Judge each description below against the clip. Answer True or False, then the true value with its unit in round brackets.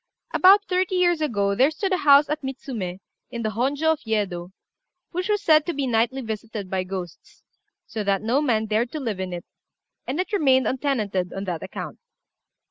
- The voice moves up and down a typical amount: False (7.2 semitones)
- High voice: True (245 Hz)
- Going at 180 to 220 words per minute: True (190 wpm)